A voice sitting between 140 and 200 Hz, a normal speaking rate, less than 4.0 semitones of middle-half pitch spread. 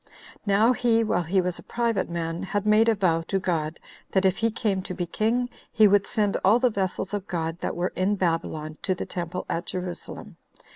No: high, 190 Hz; fast, 210 wpm; average, 3.5 semitones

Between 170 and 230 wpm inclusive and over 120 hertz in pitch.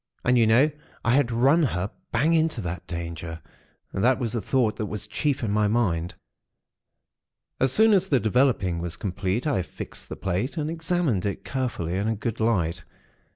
No: average, 180 wpm; low, 115 Hz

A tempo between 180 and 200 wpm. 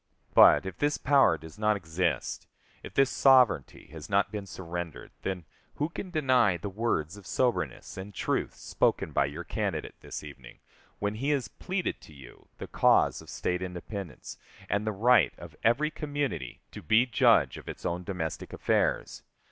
No: average, 170 wpm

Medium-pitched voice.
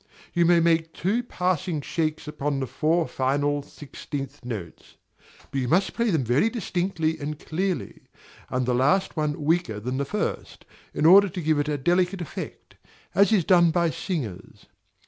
Yes: medium, 160 Hz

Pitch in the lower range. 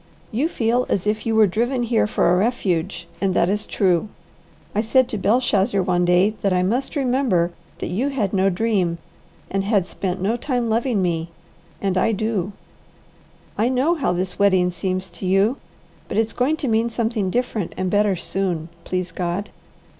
No: high, 200 Hz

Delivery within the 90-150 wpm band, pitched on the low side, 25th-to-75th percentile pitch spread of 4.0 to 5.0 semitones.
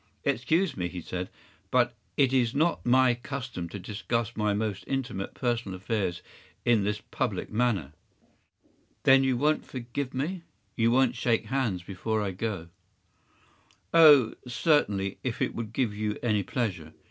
Yes: average, 145 wpm; low, 115 Hz; average, 4.5 semitones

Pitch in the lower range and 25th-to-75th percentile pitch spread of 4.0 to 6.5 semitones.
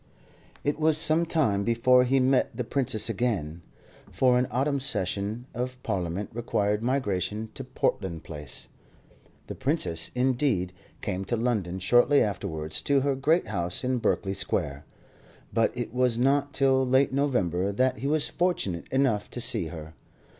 Yes: low, 120 Hz; wide, 5.5 semitones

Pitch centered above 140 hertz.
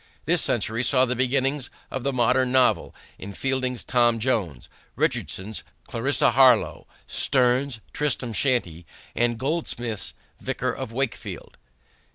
No: low, 125 Hz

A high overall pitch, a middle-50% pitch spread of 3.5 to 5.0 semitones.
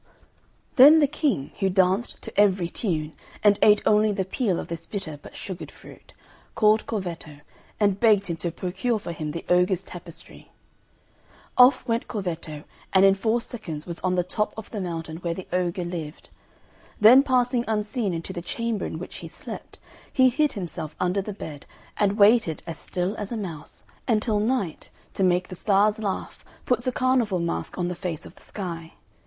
Yes: high, 195 Hz; average, 4.1 semitones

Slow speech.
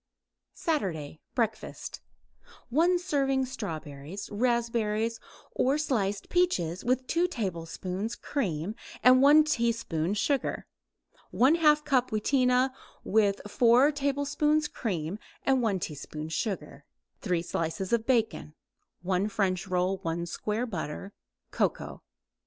Yes: slow, 100 wpm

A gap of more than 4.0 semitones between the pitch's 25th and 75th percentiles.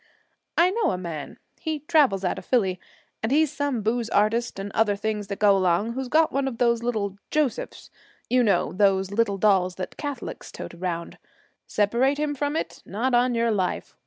Yes: average, 5.2 semitones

